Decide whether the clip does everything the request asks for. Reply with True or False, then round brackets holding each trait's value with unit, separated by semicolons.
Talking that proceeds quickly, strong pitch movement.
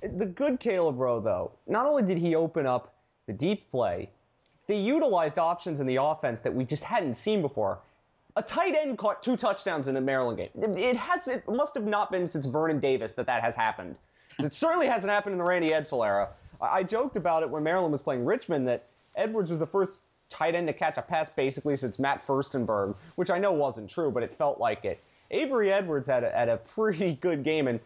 True (225 wpm; 7.5 semitones)